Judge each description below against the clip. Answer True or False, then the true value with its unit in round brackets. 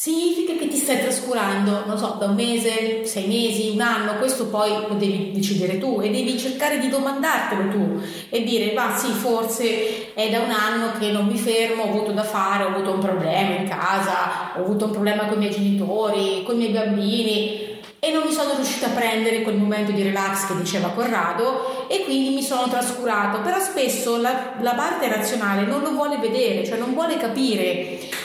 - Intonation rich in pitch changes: False (3.3 semitones)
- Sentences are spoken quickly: True (200 wpm)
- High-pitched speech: True (225 Hz)